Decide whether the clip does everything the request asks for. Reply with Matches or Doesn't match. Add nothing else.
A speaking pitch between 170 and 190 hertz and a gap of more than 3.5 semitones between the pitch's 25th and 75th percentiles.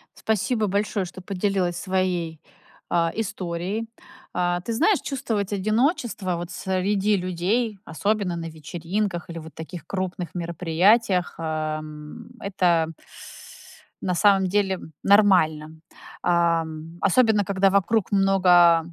Doesn't match